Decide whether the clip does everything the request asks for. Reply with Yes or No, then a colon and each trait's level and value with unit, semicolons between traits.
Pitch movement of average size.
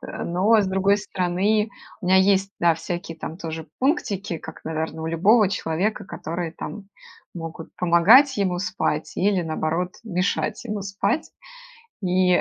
Yes: average, 3.2 semitones